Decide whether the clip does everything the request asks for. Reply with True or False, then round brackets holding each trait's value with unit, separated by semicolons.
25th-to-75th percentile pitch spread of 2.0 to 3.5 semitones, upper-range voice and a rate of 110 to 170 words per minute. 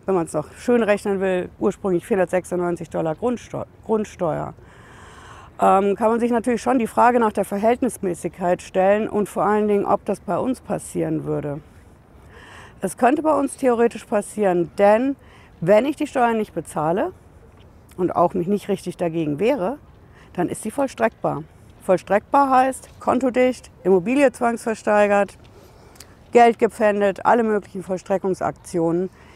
False (5.0 semitones; 200 Hz; 135 wpm)